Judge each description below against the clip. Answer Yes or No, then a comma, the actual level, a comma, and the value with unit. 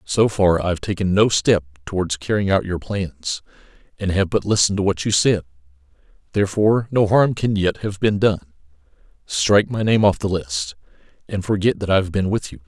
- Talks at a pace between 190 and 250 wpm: Yes, average, 200 wpm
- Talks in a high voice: No, very low, 95 Hz